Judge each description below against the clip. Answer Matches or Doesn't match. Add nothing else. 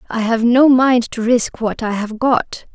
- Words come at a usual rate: Doesn't match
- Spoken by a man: Doesn't match